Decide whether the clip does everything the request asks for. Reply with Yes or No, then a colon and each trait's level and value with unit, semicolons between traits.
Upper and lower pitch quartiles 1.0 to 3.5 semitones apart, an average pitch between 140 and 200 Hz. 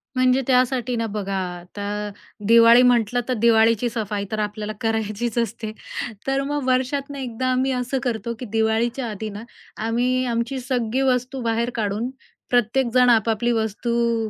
No: narrow, 2.4 semitones; high, 235 Hz